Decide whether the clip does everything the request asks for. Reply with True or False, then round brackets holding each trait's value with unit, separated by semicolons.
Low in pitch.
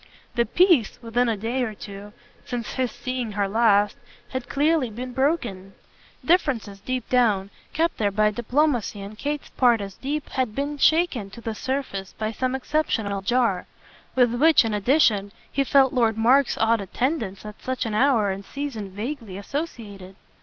False (235 Hz)